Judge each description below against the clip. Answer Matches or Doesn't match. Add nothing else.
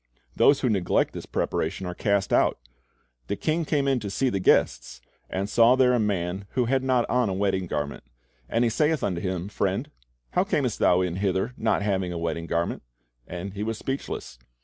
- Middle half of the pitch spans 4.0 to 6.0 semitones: Matches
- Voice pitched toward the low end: Matches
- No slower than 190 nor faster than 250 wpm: Matches